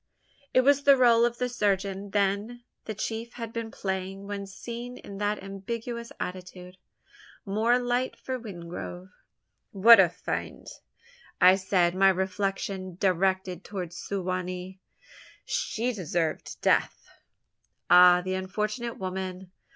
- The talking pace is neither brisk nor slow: No, slow, 130 wpm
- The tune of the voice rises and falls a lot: No, average, 3.7 semitones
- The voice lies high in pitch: Yes, high, 195 Hz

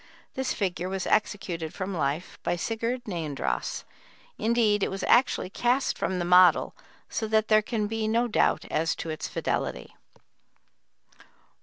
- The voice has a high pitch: Yes, high, 205 Hz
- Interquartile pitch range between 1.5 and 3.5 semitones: No, average, 4.3 semitones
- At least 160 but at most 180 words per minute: No, average, 145 wpm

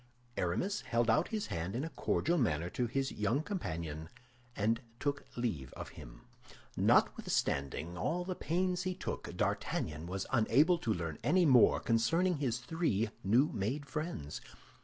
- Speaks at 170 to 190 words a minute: No, average, 150 wpm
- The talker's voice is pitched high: No, low, 120 Hz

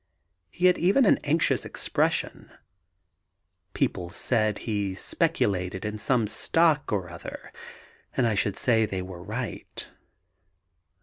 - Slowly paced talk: Yes, slow, 120 wpm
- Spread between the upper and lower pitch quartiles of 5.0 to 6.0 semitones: Yes, wide, 5.5 semitones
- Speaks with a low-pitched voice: Yes, low, 105 Hz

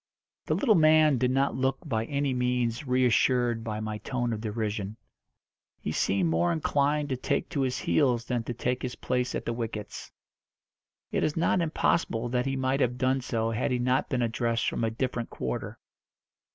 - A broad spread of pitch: No, average, 2.7 semitones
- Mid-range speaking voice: No, low, 125 Hz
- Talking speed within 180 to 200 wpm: Yes, average, 185 wpm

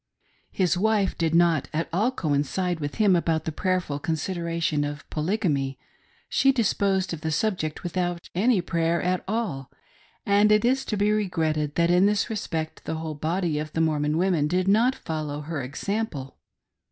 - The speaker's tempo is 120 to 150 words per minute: No, average, 165 wpm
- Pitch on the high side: No, medium, 170 Hz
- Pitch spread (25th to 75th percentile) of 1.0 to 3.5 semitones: No, average, 4.3 semitones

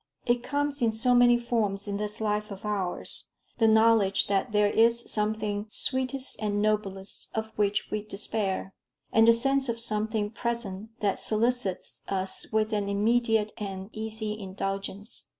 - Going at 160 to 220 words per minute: No, average, 150 wpm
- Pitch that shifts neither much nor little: No, narrow, 2.3 semitones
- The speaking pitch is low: No, high, 215 Hz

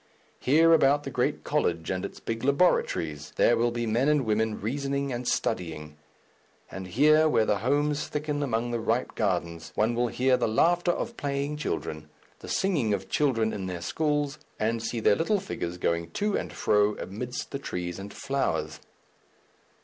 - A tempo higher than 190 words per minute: No, average, 170 wpm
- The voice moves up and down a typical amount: No, wide, 6.1 semitones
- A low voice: Yes, low, 120 Hz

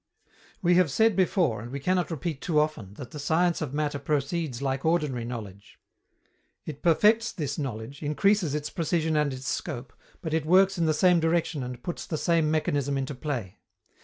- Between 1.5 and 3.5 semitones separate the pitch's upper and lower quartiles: No, average, 4.1 semitones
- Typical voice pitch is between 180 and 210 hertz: No, medium, 150 Hz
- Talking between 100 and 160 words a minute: No, average, 185 wpm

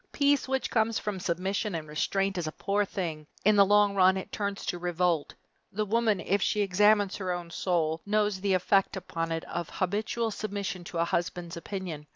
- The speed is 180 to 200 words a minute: Yes, average, 195 wpm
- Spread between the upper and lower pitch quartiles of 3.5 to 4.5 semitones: No, average, 3.0 semitones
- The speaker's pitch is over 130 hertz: Yes, high, 190 Hz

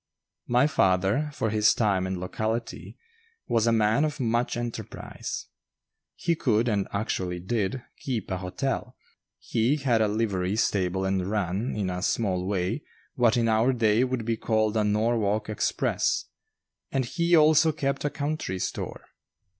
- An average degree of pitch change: Yes, average, 4.0 semitones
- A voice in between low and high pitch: No, low, 110 Hz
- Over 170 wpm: No, average, 150 wpm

